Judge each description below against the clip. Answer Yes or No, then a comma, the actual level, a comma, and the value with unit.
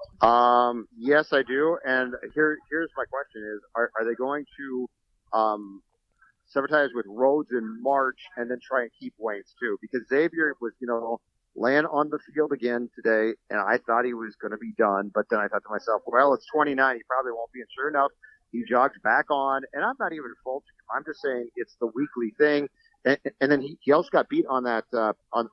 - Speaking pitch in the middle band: No, low, 130 Hz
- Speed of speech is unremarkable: No, fast, 215 wpm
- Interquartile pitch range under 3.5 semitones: No, average, 4.1 semitones